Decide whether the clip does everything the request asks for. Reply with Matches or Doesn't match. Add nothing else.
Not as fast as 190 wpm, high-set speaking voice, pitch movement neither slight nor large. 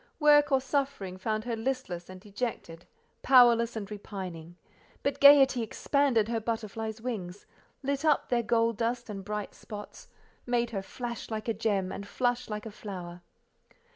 Matches